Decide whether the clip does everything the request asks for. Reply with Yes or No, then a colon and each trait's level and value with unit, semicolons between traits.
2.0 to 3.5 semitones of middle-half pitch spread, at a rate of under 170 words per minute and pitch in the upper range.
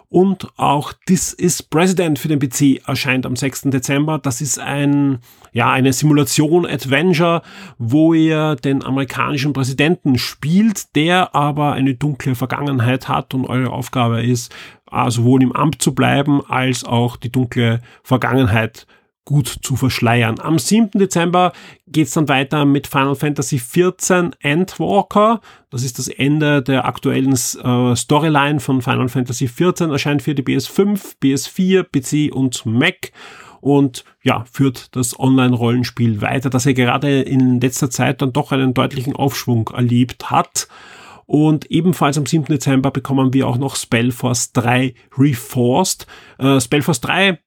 No: average, 2.9 semitones; average, 150 wpm; low, 135 Hz